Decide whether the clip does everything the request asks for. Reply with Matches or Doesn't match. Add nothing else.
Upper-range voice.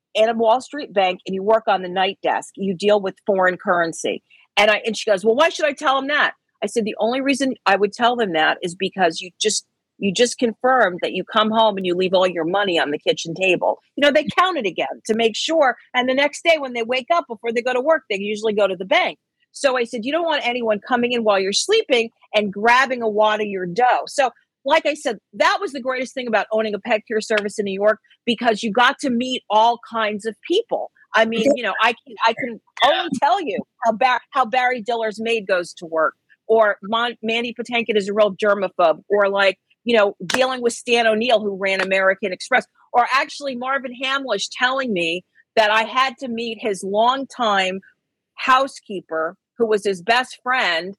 Matches